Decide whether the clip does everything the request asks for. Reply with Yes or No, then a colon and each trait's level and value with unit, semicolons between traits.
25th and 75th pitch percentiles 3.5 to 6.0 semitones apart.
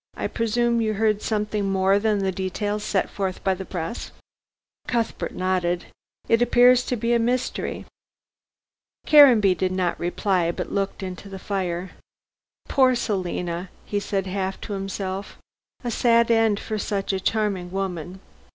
No: average, 3.1 semitones